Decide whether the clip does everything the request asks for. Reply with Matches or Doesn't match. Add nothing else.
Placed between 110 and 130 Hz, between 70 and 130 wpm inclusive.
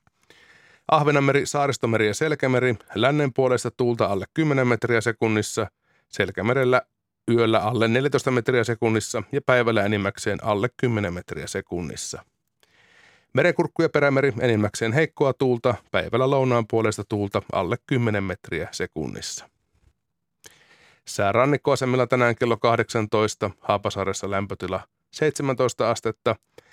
Matches